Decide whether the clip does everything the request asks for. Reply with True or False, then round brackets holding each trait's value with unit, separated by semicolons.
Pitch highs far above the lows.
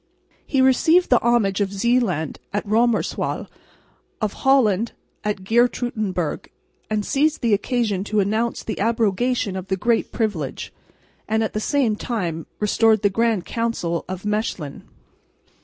False (3.4 semitones)